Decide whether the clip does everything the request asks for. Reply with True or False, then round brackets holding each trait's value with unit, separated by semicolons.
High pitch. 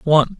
False (150 Hz)